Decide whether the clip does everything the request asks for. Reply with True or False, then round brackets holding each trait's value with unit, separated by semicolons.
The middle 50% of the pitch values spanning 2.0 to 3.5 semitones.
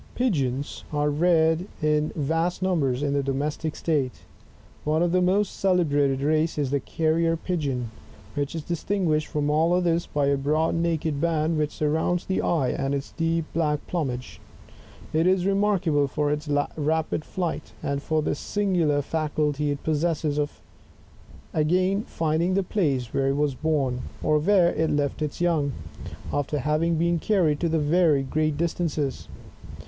True (2.7 semitones)